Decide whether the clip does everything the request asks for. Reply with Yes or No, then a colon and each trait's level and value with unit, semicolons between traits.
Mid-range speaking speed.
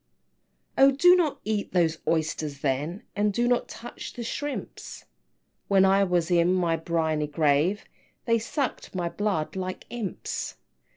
Yes: average, 150 wpm